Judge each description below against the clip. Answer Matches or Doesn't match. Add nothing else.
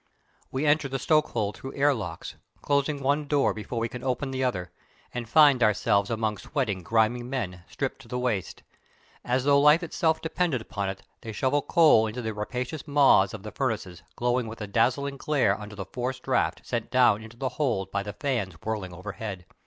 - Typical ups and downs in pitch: Matches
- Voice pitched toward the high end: Doesn't match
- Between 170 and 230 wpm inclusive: Matches